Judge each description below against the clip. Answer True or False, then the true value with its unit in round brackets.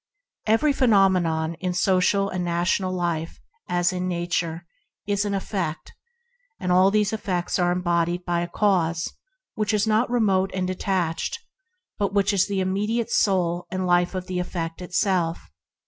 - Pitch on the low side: False (185 Hz)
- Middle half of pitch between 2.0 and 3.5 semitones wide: True (2.4 semitones)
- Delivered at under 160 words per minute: True (140 wpm)